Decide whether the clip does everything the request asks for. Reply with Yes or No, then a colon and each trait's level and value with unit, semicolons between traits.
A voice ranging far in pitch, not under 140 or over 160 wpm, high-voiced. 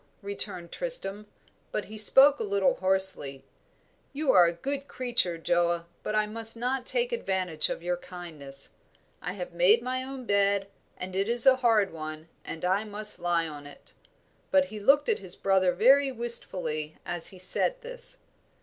No: wide, 6.3 semitones; average, 170 wpm; high, 200 Hz